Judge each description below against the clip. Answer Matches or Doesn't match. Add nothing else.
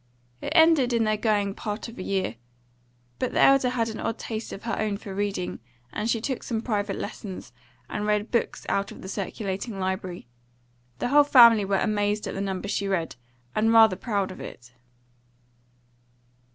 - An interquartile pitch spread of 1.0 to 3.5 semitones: Matches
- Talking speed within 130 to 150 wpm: Doesn't match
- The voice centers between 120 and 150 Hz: Doesn't match